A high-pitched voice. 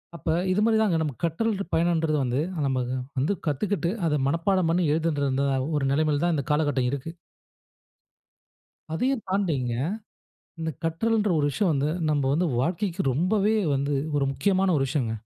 No: medium, 160 Hz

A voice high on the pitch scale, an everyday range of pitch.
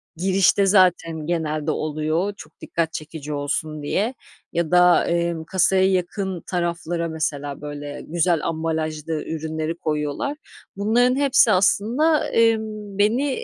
No: medium, 170 Hz; average, 4.2 semitones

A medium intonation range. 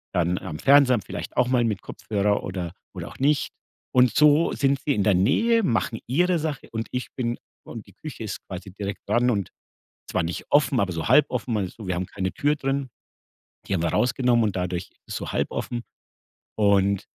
No: wide, 5.9 semitones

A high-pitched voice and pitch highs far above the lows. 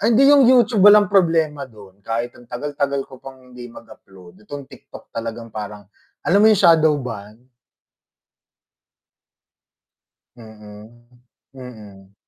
No: low, 125 Hz; wide, 7.0 semitones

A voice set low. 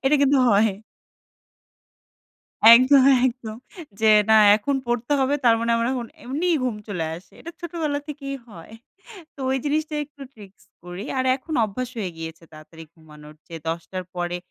No: high, 230 Hz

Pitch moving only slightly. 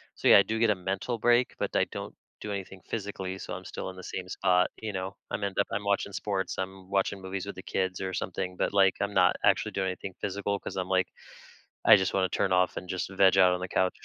Yes: narrow, 1.4 semitones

